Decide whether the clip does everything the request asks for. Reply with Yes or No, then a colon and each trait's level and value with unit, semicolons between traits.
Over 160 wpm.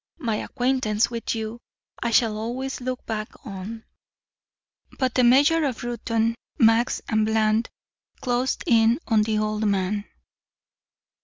No: slow, 135 wpm